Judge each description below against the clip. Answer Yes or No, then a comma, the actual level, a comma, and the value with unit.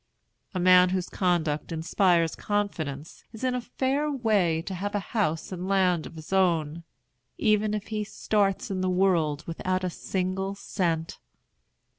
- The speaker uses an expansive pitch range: No, average, 3.5 semitones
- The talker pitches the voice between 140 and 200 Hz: Yes, medium, 185 Hz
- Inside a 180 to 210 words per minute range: No, average, 150 wpm